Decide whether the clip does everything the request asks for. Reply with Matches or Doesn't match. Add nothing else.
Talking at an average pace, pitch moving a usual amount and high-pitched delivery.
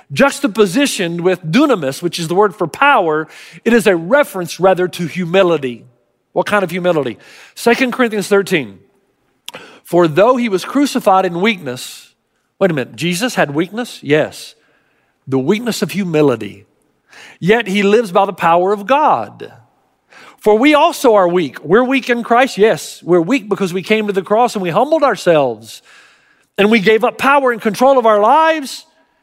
Doesn't match